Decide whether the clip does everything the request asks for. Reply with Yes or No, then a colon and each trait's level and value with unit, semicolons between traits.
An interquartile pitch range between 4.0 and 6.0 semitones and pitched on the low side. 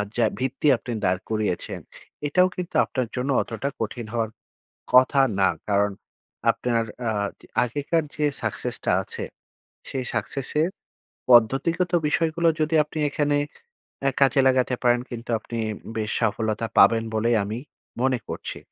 Yes: average, 4.3 semitones; low, 125 Hz